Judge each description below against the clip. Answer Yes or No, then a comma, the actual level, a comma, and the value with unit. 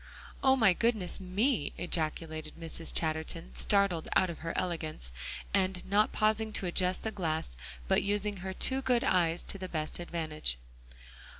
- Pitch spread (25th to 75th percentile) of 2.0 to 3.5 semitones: No, average, 4.2 semitones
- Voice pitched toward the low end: No, medium, 180 Hz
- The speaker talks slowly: No, average, 155 wpm